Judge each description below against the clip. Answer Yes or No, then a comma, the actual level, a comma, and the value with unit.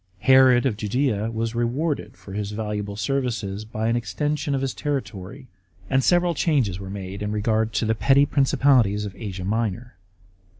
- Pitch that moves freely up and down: No, average, 4.5 semitones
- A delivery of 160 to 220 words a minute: Yes, average, 165 wpm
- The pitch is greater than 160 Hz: No, low, 115 Hz